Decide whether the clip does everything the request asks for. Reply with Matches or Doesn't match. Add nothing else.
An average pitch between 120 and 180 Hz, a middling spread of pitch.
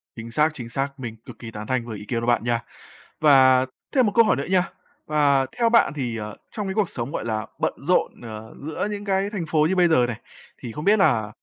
Doesn't match